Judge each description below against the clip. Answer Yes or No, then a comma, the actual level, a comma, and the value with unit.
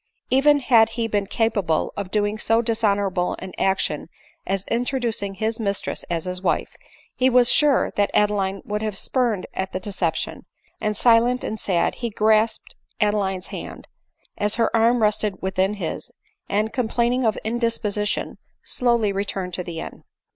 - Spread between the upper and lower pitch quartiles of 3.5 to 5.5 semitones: No, average, 3.0 semitones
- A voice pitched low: No, high, 210 Hz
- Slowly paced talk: No, average, 155 wpm